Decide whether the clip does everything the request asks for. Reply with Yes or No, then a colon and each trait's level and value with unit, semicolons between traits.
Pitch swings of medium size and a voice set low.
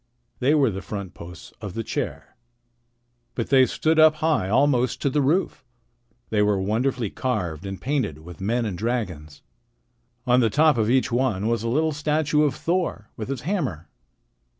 No: wide, 6.2 semitones; low, 120 Hz